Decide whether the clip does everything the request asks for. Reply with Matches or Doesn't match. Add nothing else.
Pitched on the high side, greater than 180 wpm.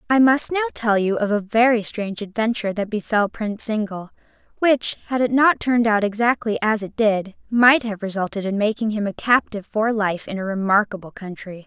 Matches